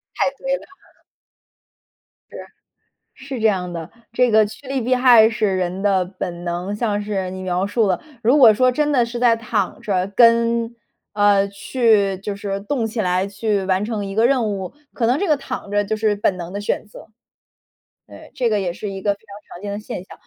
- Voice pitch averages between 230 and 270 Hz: No, high, 210 Hz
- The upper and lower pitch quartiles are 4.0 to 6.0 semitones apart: No, average, 3.2 semitones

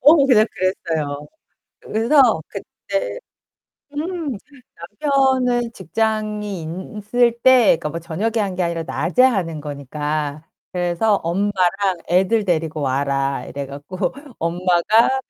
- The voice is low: No, medium, 185 Hz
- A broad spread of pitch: Yes, wide, 6.2 semitones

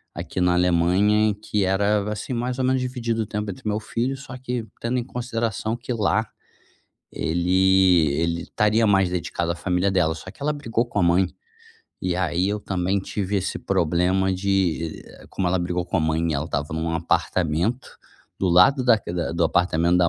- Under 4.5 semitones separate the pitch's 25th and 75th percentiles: Yes, average, 4.1 semitones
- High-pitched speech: No, very low, 95 Hz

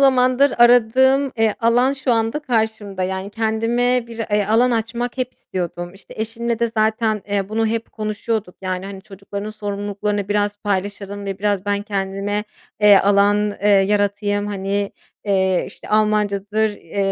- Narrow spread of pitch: Yes, narrow, 2.1 semitones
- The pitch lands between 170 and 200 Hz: No, high, 210 Hz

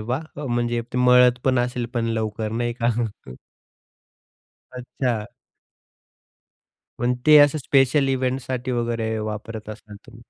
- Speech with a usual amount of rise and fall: No, narrow, 2.1 semitones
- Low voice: Yes, low, 120 Hz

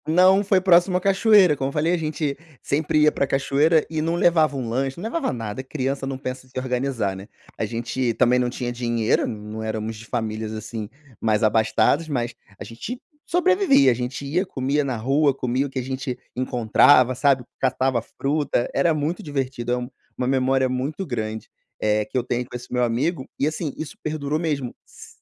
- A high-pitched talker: No, low, 130 Hz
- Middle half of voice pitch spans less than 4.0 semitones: No, average, 4.3 semitones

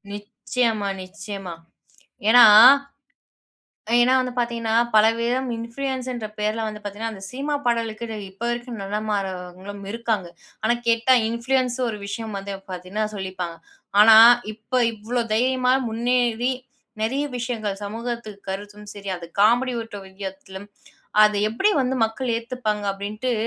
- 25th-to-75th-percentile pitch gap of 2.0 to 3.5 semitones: Yes, average, 3.1 semitones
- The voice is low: No, high, 225 Hz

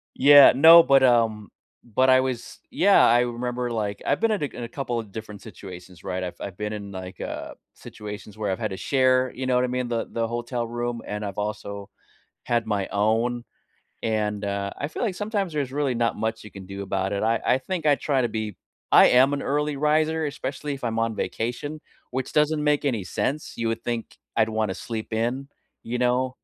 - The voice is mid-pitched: No, low, 120 Hz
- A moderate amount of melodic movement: Yes, average, 4.1 semitones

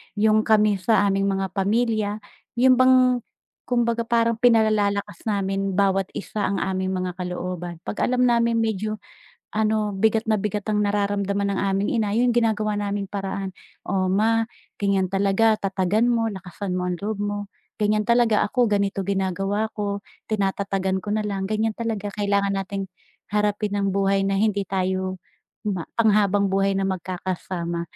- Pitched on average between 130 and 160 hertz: No, high, 200 Hz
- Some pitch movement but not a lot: No, narrow, 2.0 semitones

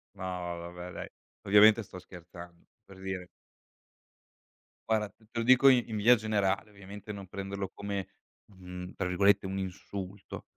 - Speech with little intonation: Yes, narrow, 2.3 semitones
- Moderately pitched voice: No, very low, 95 Hz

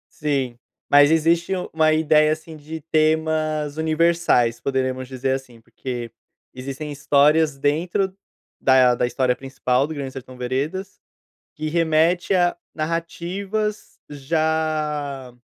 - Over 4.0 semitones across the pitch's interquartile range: No, average, 3.3 semitones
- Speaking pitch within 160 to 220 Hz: No, medium, 150 Hz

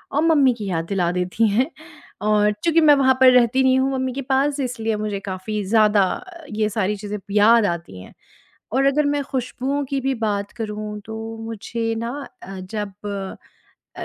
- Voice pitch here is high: Yes, high, 225 Hz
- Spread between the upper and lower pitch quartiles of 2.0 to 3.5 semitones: No, average, 4.3 semitones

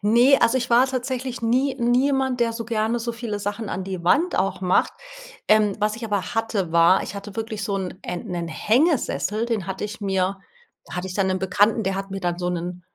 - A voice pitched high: Yes, high, 210 Hz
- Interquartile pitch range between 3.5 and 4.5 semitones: Yes, average, 3.9 semitones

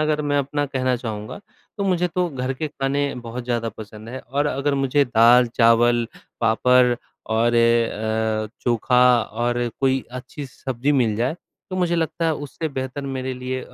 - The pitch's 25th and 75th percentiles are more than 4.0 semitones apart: No, average, 3.3 semitones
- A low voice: Yes, low, 125 Hz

